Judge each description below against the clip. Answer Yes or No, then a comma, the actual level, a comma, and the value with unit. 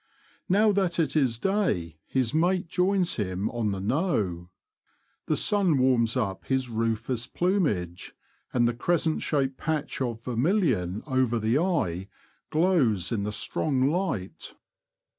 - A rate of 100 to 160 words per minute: Yes, average, 140 wpm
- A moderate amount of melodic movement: No, wide, 7.7 semitones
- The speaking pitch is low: Yes, low, 130 Hz